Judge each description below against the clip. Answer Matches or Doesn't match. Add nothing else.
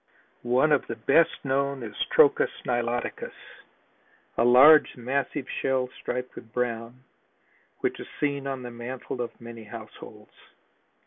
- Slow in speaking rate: Matches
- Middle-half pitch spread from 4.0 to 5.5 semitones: Doesn't match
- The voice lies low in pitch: Matches